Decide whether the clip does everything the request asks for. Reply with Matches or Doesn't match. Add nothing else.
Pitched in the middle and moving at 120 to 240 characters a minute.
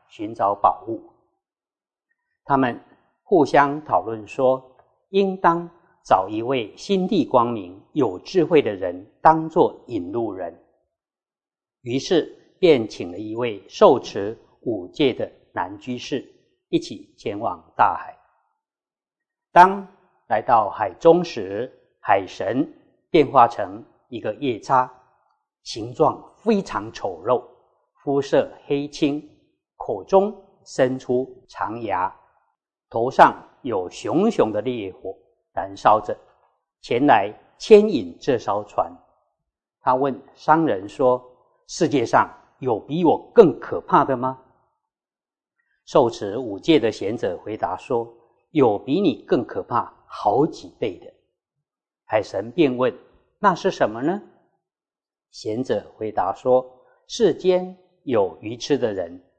Matches